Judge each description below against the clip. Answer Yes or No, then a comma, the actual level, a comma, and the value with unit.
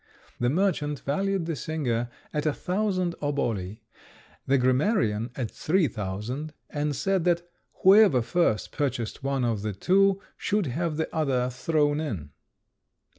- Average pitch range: No, wide, 6.1 semitones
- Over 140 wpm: No, slow, 135 wpm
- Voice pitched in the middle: Yes, medium, 145 Hz